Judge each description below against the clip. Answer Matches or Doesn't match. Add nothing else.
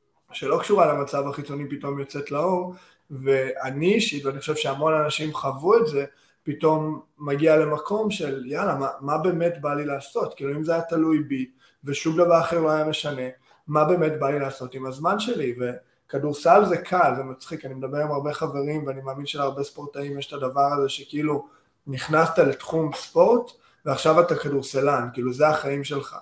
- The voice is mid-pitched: Matches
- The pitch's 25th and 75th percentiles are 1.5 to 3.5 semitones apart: Matches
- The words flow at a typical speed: Doesn't match